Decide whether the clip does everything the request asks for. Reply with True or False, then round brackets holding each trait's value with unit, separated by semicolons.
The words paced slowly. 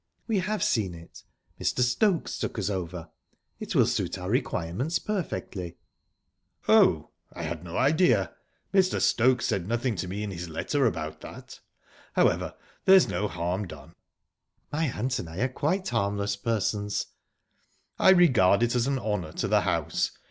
False (155 wpm)